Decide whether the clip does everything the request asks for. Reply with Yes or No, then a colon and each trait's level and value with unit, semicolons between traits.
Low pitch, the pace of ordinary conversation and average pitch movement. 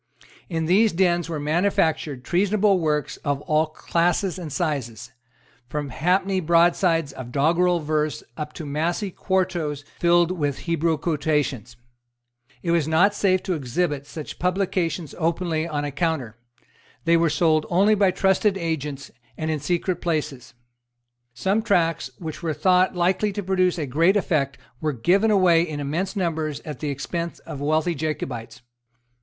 No: medium, 165 Hz; average, 150 wpm; average, 3.4 semitones